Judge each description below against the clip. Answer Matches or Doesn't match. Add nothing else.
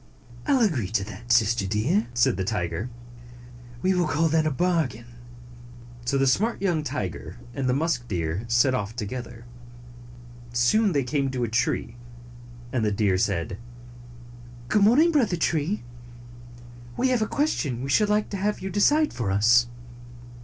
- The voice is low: Matches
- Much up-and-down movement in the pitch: Matches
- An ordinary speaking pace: Matches